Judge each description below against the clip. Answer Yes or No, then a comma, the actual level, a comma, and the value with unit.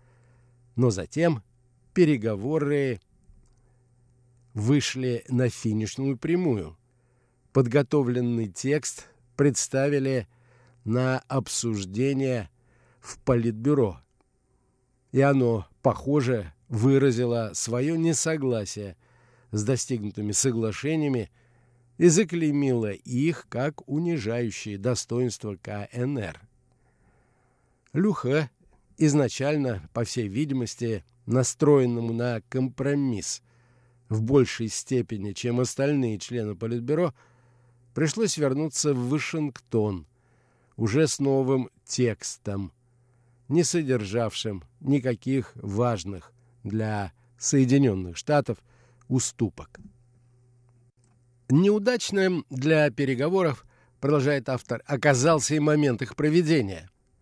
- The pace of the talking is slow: Yes, slow, 75 wpm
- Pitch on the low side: Yes, low, 125 Hz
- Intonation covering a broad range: No, average, 3.0 semitones